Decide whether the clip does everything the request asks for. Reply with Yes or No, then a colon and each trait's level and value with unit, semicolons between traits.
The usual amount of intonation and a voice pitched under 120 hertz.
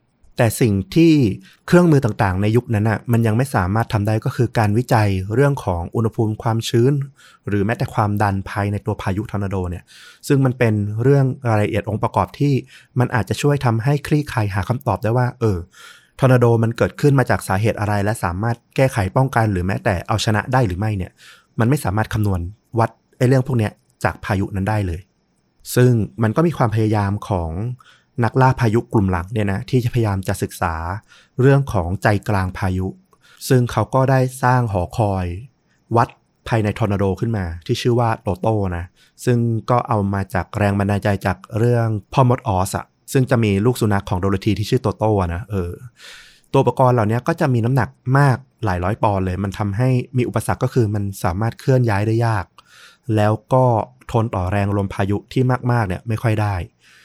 Yes: average, 3.7 semitones; low, 110 Hz